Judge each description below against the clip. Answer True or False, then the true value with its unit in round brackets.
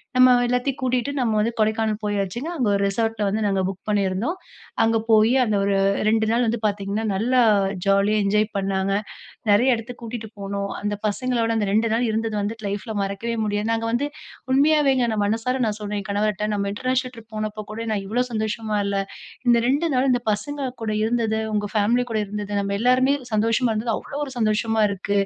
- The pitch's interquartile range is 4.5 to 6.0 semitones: False (2.9 semitones)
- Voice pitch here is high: True (220 Hz)